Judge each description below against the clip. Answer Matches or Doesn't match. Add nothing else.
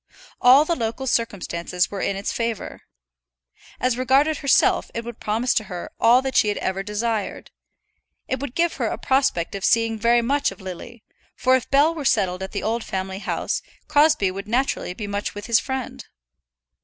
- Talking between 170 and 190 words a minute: Matches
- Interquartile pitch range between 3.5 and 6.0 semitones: Matches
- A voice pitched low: Doesn't match